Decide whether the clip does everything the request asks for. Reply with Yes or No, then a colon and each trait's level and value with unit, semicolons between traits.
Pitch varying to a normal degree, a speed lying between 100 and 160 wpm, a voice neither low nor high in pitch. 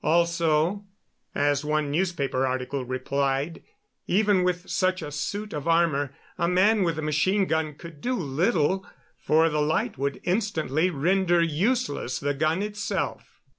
Yes: average, 4.3 semitones; average, 140 wpm; medium, 160 Hz